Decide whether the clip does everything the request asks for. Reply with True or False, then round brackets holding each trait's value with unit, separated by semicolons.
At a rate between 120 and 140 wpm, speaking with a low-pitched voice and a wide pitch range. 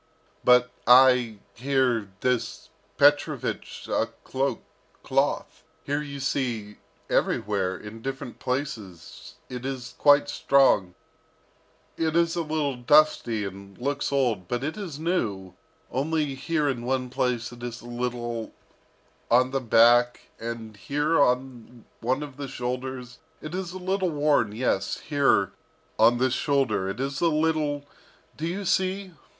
False (135 wpm; 130 Hz; 3.6 semitones)